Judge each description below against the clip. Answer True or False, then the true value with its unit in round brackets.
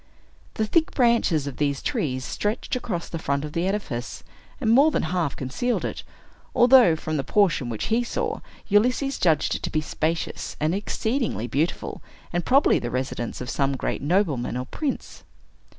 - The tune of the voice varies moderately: False (8.5 semitones)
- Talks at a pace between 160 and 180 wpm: True (170 wpm)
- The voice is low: False (170 Hz)